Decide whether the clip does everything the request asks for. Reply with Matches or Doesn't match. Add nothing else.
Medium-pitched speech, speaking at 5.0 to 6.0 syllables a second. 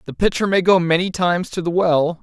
Matches